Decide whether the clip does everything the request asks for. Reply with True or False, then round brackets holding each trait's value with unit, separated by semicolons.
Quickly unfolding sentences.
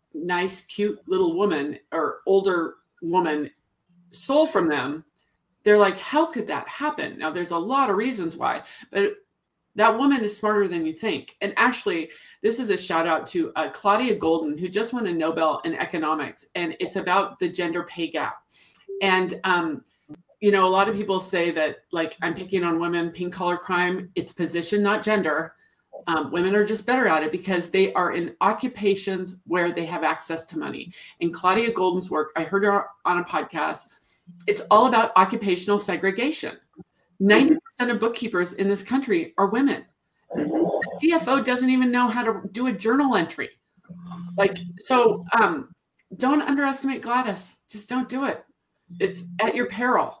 False (175 wpm)